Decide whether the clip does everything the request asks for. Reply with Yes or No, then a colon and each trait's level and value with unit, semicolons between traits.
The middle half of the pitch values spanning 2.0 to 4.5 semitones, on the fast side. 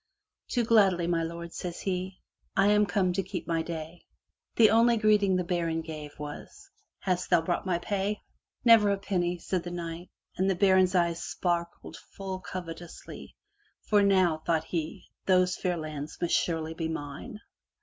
No: average, 2.8 semitones; average, 165 wpm